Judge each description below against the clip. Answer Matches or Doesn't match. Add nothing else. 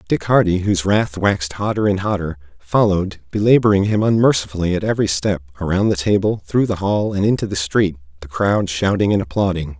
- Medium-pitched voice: Doesn't match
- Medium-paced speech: Matches